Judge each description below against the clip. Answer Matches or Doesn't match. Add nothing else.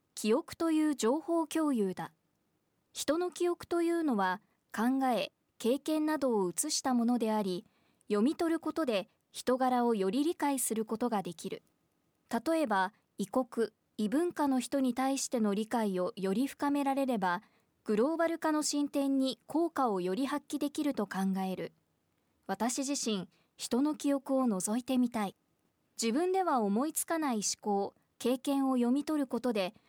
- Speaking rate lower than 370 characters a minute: Matches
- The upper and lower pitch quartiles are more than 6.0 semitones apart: Doesn't match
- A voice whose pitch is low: Doesn't match